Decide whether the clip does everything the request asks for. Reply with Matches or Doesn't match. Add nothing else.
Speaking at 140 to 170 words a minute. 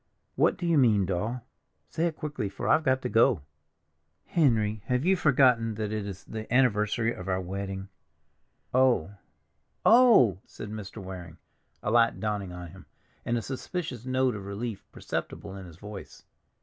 Matches